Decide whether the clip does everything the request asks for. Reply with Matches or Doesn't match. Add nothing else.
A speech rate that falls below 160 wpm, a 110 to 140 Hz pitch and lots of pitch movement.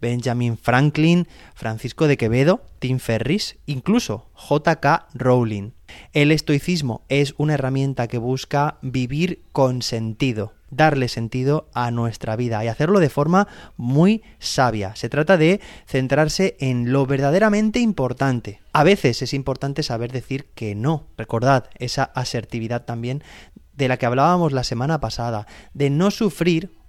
Doesn't match